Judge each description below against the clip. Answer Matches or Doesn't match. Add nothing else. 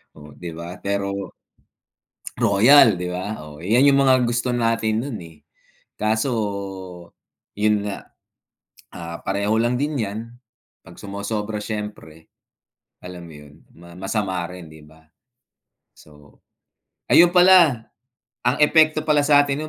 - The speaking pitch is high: Doesn't match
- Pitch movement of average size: Doesn't match